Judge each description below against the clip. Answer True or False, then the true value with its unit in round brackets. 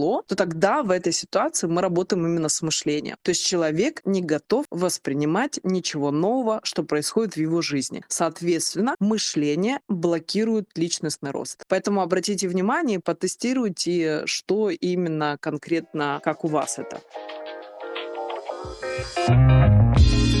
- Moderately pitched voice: True (175 Hz)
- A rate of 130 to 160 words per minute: False (115 wpm)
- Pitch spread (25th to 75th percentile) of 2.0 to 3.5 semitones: False (3.9 semitones)